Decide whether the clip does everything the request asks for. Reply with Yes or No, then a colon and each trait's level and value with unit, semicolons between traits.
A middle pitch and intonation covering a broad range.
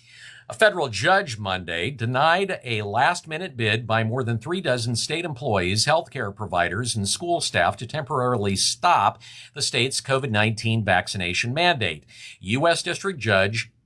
No: low, 120 Hz; wide, 5.7 semitones